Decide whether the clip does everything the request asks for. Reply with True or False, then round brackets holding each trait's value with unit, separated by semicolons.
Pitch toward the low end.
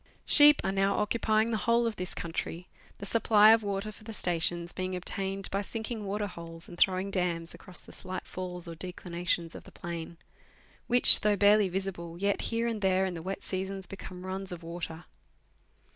False (190 Hz)